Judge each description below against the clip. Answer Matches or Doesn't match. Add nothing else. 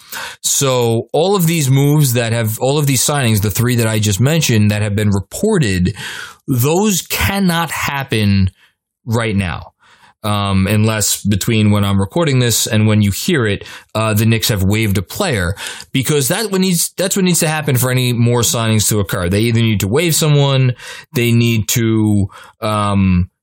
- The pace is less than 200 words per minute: Matches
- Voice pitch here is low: Matches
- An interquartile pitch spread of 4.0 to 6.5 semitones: Matches